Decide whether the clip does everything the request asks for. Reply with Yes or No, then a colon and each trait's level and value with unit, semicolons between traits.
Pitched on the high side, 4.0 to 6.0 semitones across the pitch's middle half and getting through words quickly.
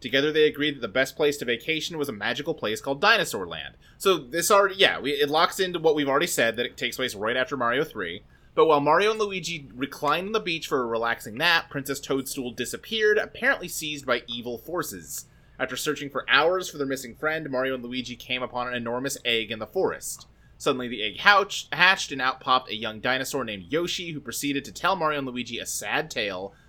No: medium, 140 Hz; average, 4.6 semitones; fast, 220 wpm